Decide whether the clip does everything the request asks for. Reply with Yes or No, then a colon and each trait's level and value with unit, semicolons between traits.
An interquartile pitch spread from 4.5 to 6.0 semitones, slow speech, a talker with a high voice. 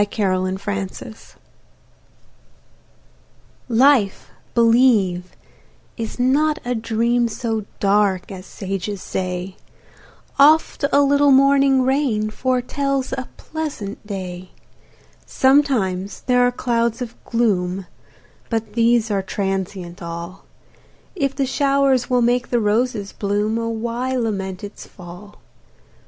Yes: average, 4.8 semitones; slow, 110 wpm; high, 225 Hz